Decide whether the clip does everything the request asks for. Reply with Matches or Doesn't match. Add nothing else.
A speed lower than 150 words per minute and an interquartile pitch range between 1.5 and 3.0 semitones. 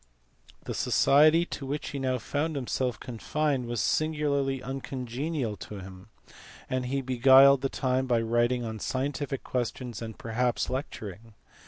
Matches